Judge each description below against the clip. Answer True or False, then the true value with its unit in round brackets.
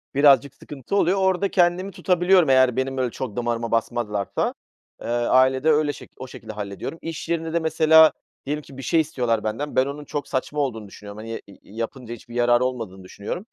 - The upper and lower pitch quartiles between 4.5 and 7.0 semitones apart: True (5.3 semitones)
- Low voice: True (130 Hz)